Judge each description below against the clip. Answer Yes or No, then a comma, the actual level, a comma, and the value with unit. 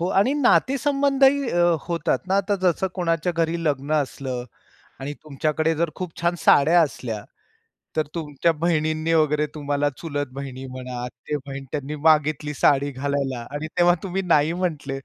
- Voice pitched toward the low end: No, medium, 155 Hz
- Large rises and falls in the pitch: No, average, 3.6 semitones